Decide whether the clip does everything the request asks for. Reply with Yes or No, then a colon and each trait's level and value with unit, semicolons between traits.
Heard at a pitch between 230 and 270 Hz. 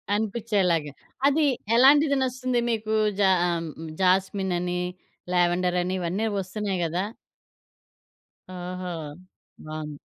No: medium, 185 Hz